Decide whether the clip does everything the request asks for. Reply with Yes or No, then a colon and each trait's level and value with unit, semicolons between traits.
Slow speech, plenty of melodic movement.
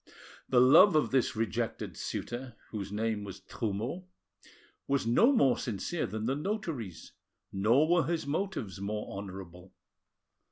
Yes: slow, 130 wpm; wide, 7.1 semitones